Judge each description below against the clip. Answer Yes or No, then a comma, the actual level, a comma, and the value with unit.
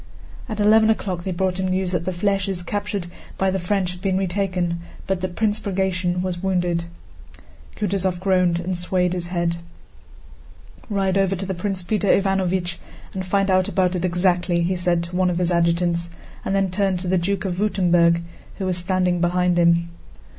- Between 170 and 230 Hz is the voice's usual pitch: Yes, medium, 185 Hz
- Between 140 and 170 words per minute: No, average, 180 wpm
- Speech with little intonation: Yes, narrow, 1.7 semitones